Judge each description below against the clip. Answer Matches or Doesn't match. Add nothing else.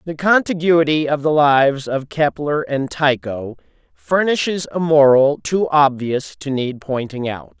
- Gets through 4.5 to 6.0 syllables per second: Doesn't match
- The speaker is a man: Matches